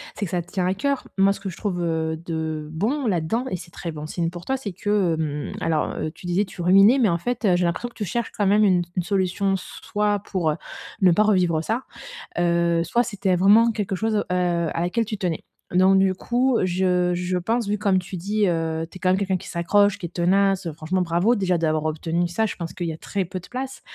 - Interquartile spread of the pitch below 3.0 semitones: No, average, 3.3 semitones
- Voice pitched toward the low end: No, medium, 185 Hz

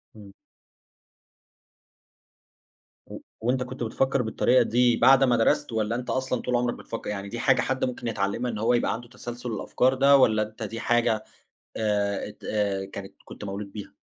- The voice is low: Yes, low, 115 Hz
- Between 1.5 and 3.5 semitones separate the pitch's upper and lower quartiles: Yes, average, 2.9 semitones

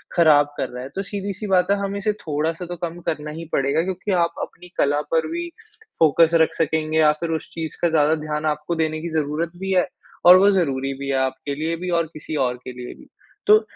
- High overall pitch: No, medium, 160 Hz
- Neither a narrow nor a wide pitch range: Yes, average, 3.1 semitones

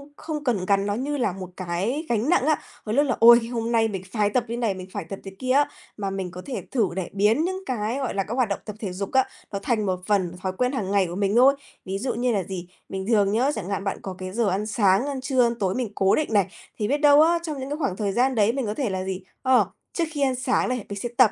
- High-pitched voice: Yes, high, 220 Hz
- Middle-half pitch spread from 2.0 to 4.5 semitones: No, average, 4.9 semitones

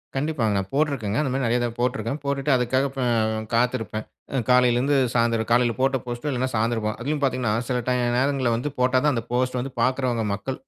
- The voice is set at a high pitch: No, low, 125 Hz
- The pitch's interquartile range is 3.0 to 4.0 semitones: No, narrow, 2.5 semitones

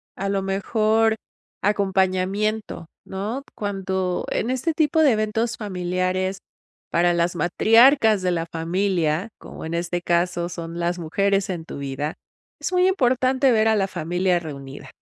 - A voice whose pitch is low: No, high, 190 Hz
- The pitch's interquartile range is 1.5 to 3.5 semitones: No, average, 4.1 semitones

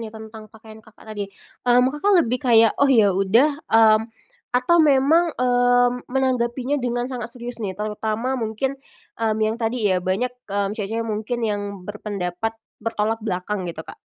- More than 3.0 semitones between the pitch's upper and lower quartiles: No, average, 2.7 semitones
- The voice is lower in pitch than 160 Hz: No, high, 225 Hz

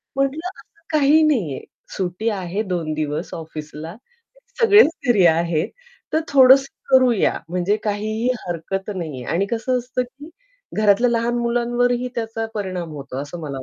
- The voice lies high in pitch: Yes, high, 215 Hz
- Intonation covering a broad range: Yes, wide, 6.5 semitones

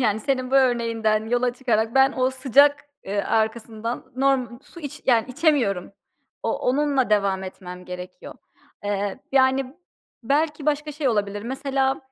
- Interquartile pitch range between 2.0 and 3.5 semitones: No, average, 4.0 semitones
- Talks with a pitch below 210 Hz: No, very high, 250 Hz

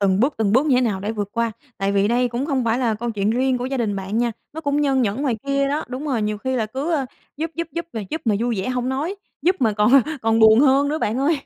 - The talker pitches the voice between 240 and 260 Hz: Yes, high, 245 Hz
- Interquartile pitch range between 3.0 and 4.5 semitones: Yes, average, 4.1 semitones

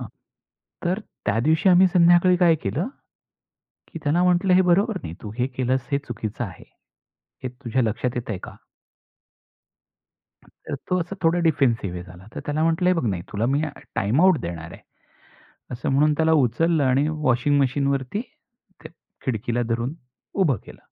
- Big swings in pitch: Yes, wide, 5.9 semitones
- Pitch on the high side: No, medium, 140 Hz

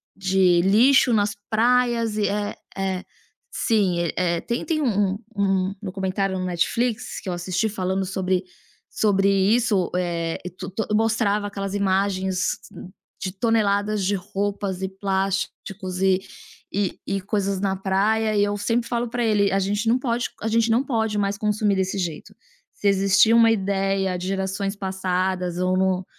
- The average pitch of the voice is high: Yes, high, 195 Hz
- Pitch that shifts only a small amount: Yes, narrow, 2.1 semitones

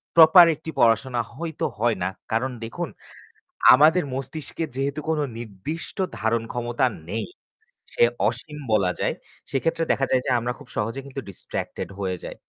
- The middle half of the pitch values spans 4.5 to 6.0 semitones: Yes, average, 5.1 semitones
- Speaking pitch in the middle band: No, low, 130 Hz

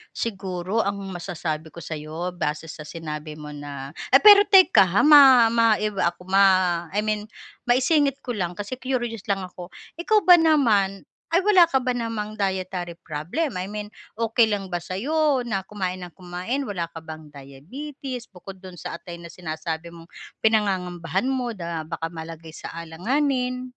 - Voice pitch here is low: No, high, 190 Hz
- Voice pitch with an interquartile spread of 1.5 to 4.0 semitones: No, wide, 6.3 semitones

